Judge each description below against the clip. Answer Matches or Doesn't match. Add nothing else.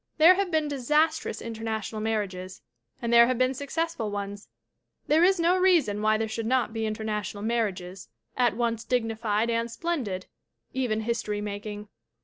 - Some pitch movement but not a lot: Matches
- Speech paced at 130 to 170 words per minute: Matches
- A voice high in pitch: Matches